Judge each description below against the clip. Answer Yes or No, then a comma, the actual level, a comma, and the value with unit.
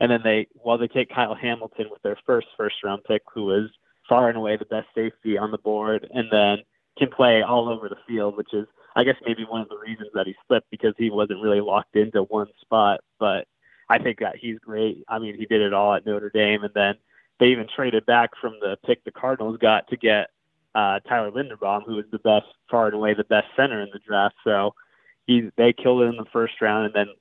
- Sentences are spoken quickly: Yes, fast, 240 wpm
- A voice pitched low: Yes, low, 110 Hz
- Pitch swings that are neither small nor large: No, narrow, 1.9 semitones